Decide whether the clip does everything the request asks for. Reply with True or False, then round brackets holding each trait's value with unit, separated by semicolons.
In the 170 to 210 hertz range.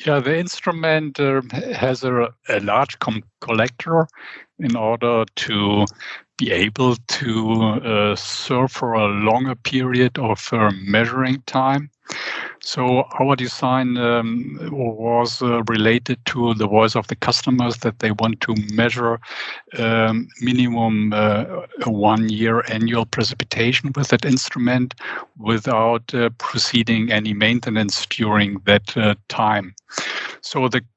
False (115 Hz)